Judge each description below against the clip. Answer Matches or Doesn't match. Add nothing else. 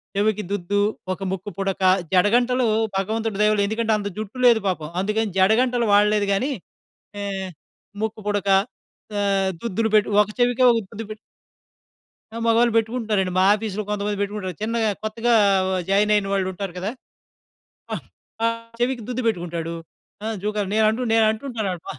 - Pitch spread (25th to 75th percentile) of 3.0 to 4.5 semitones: Doesn't match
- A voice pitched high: Matches